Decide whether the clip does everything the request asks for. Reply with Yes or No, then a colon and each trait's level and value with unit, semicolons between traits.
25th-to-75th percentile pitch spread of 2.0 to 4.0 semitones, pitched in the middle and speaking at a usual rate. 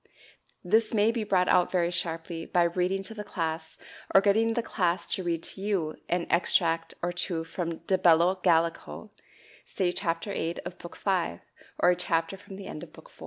Yes: narrow, 2.6 semitones; medium, 175 Hz; average, 195 wpm